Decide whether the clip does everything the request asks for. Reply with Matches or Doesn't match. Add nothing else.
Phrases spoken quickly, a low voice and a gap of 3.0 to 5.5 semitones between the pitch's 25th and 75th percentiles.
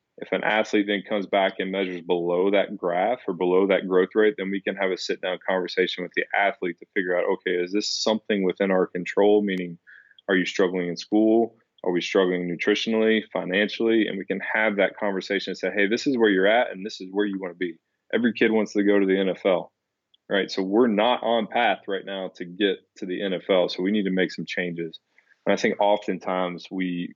Doesn't match